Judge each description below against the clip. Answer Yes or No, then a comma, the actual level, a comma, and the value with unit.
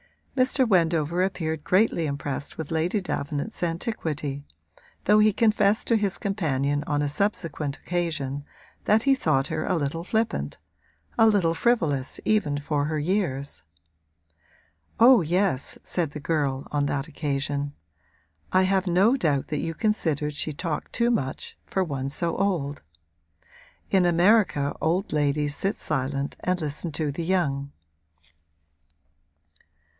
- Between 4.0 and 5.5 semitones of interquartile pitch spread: Yes, average, 5.1 semitones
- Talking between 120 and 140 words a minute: Yes, slow, 135 wpm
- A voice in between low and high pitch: Yes, medium, 160 Hz